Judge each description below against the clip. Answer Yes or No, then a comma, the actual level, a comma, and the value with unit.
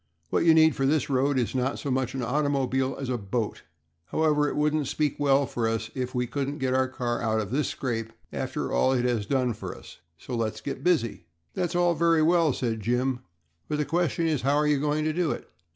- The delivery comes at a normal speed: No, fast, 230 wpm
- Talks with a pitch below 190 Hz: Yes, low, 135 Hz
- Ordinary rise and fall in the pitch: Yes, average, 3.6 semitones